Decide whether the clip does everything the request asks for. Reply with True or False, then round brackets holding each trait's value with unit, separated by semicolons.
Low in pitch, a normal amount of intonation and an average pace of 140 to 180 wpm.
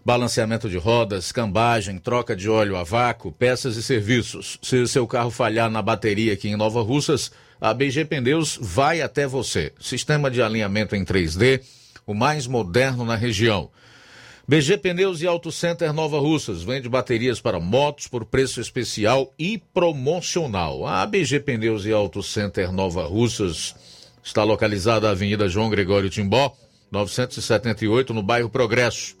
True (120 Hz; 3.6 semitones; 150 wpm)